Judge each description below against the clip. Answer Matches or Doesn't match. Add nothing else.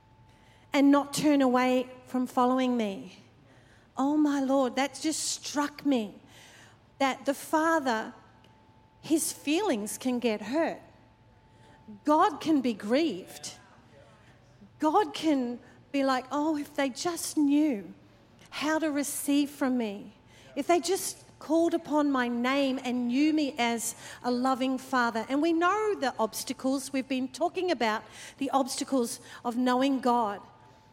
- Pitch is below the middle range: Doesn't match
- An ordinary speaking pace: Doesn't match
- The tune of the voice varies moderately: Matches